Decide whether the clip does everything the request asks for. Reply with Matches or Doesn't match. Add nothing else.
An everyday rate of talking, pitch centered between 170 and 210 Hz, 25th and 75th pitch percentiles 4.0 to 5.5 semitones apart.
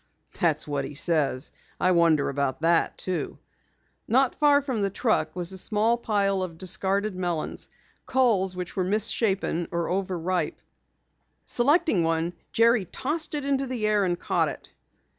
Matches